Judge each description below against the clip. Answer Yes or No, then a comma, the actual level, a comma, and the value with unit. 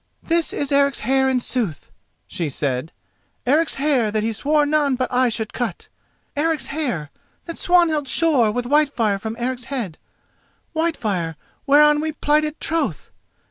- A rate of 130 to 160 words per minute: Yes, average, 140 wpm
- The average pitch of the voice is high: Yes, very high, 265 Hz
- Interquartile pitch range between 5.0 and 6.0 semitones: Yes, average, 5.3 semitones